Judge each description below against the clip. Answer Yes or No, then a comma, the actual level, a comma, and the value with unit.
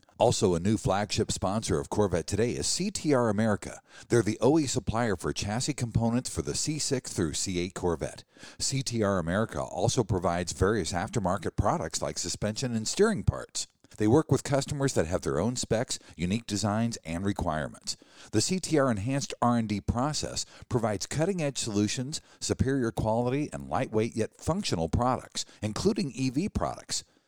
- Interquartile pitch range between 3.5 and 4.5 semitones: No, average, 4.9 semitones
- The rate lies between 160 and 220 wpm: No, average, 145 wpm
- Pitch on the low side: Yes, low, 110 Hz